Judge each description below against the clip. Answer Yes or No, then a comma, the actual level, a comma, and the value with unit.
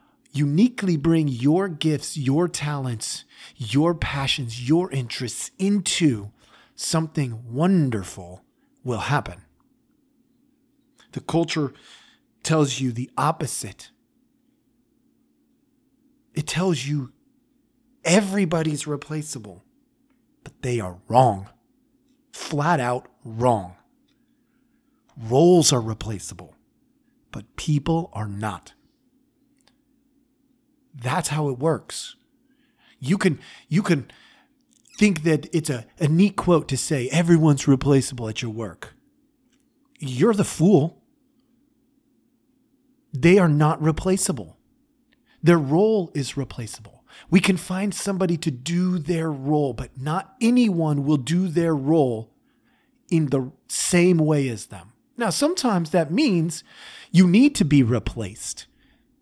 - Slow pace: Yes, slow, 105 wpm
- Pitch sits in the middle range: Yes, medium, 170 Hz